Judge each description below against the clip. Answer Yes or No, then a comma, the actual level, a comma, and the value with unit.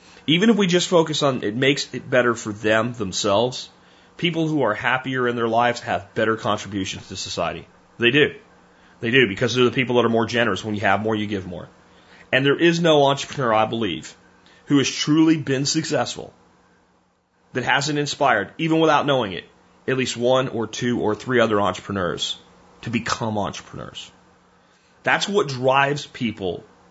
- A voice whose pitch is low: Yes, low, 115 Hz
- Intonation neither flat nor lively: No, wide, 6.6 semitones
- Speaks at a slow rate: No, average, 175 wpm